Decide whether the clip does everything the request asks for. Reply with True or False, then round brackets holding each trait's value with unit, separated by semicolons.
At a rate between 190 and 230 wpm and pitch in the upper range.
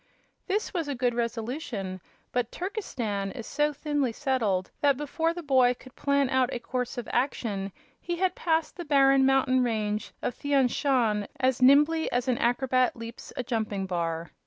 False (170 wpm; 255 Hz)